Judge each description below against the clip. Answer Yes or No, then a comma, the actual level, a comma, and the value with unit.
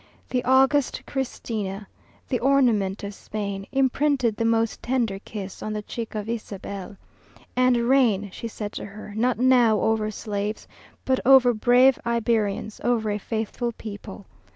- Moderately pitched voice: No, high, 225 Hz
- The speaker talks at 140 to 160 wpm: Yes, average, 145 wpm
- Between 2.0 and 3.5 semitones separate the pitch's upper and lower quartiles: Yes, average, 3.2 semitones